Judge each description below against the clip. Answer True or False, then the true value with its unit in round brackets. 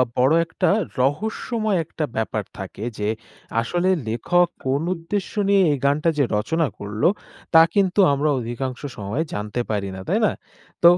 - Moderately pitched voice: True (145 Hz)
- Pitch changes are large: True (7.9 semitones)